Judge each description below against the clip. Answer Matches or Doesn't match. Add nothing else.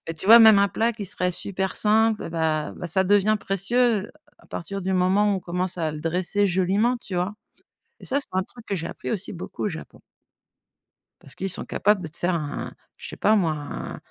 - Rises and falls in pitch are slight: Doesn't match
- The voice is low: Doesn't match